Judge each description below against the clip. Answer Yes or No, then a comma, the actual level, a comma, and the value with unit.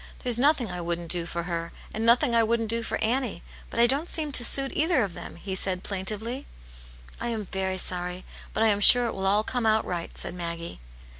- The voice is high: Yes, high, 215 Hz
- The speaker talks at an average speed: No, fast, 230 wpm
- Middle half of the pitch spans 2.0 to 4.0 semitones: No, average, 5.0 semitones